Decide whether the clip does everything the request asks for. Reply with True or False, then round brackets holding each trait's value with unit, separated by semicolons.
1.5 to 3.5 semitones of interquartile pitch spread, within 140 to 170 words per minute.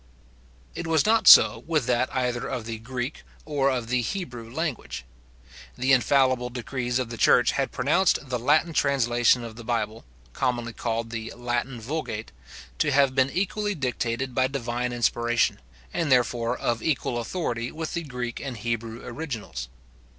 True (2.8 semitones; 160 wpm)